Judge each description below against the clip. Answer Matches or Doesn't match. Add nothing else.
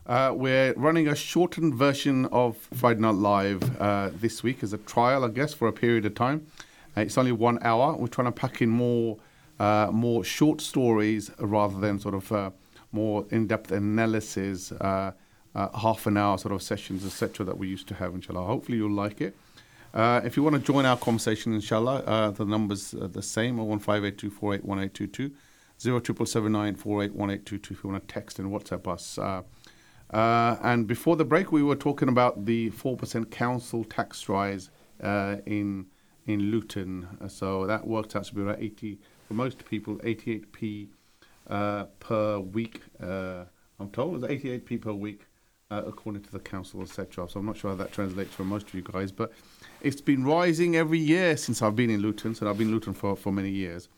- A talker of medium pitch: Doesn't match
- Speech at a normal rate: Doesn't match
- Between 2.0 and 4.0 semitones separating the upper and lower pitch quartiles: Matches